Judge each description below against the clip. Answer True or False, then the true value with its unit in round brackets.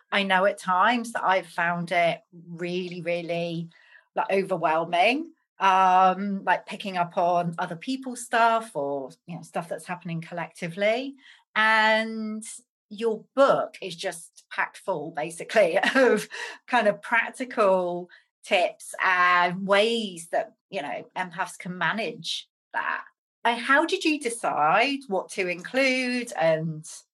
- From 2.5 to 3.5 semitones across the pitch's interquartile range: False (4.7 semitones)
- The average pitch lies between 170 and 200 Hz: True (190 Hz)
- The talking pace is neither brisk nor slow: False (130 wpm)